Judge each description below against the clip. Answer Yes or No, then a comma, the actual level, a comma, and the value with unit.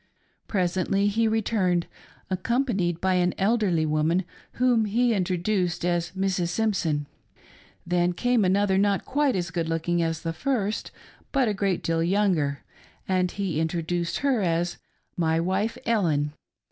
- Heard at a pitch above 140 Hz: Yes, medium, 185 Hz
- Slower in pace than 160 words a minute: Yes, average, 140 wpm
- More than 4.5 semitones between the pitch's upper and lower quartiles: No, average, 3.7 semitones